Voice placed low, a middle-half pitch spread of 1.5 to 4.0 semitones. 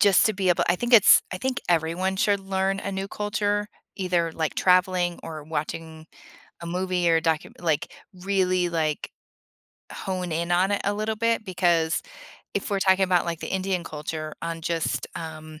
No: medium, 180 Hz; average, 2.9 semitones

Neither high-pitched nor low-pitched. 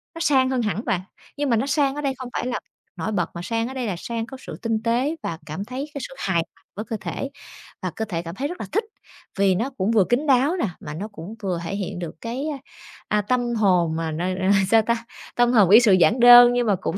No: high, 225 Hz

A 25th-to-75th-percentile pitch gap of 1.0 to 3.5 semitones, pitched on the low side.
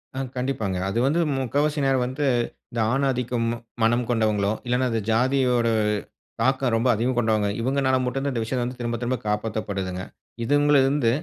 Yes: average, 2.8 semitones; low, 125 Hz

